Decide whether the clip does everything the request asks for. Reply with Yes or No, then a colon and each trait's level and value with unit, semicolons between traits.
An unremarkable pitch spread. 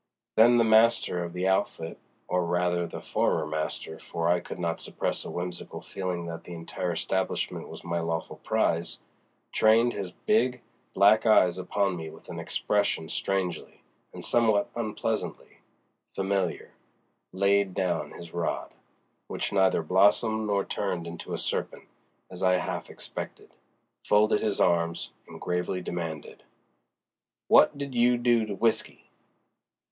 Yes: average, 3.8 semitones